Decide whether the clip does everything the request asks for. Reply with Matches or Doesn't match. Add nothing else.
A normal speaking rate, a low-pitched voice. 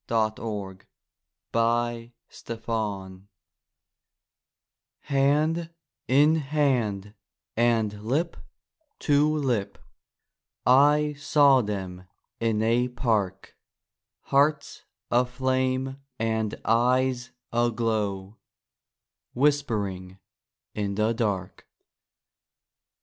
Doesn't match